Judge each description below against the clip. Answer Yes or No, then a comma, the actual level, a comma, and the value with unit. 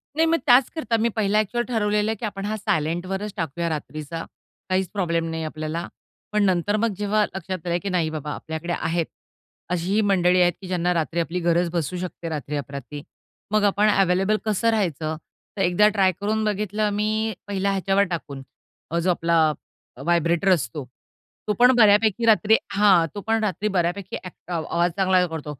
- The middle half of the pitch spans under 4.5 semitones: Yes, average, 3.8 semitones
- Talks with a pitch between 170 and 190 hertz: Yes, medium, 185 Hz